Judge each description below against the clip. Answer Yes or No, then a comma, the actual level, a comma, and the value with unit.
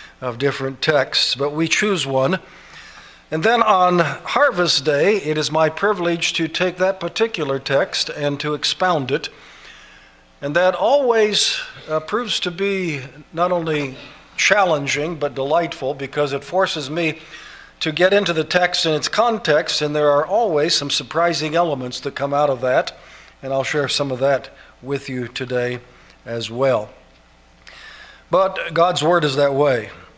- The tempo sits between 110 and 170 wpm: Yes, average, 155 wpm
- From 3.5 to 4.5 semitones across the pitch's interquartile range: Yes, average, 4.2 semitones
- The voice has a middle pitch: Yes, medium, 150 Hz